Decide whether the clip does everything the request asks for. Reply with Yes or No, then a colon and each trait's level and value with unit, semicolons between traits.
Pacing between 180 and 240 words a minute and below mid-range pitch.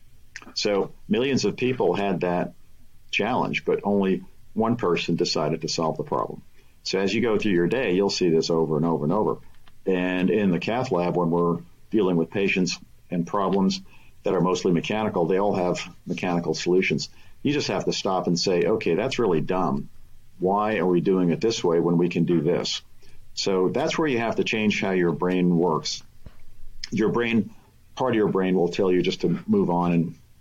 Yes: average, 195 wpm; very low, 90 Hz